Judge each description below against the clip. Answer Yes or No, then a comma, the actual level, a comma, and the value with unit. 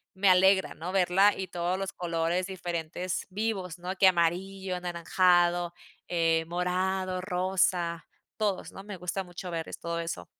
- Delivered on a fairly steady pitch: Yes, narrow, 1.7 semitones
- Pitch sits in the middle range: Yes, medium, 180 Hz